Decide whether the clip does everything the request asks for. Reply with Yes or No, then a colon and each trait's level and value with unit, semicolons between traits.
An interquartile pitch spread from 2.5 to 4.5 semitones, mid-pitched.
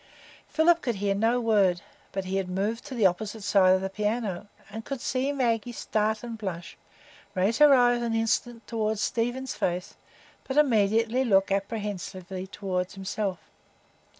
No: average, 3.7 semitones; high, 215 Hz